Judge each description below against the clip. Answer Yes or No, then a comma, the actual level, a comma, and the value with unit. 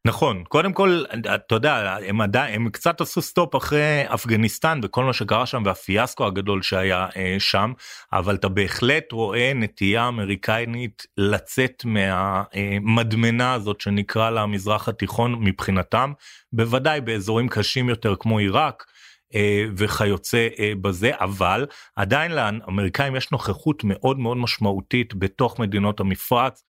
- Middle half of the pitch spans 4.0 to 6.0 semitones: No, average, 3.5 semitones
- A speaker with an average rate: Yes, average, 120 wpm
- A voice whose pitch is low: Yes, low, 110 Hz